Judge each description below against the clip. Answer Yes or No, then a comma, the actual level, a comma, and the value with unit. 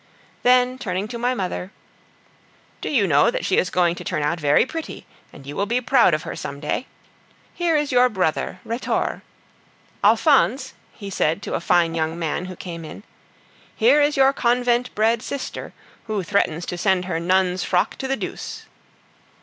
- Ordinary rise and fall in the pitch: No, wide, 6.5 semitones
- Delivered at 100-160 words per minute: No, average, 180 wpm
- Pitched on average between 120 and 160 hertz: No, high, 200 Hz